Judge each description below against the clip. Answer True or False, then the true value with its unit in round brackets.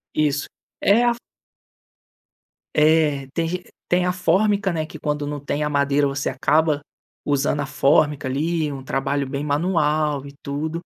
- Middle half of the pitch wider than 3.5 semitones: False (2.4 semitones)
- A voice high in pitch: False (150 Hz)